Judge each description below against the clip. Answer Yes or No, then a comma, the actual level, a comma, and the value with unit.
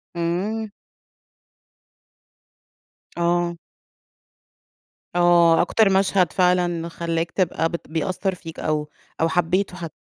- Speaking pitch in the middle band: Yes, medium, 175 Hz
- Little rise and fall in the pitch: Yes, narrow, 1.9 semitones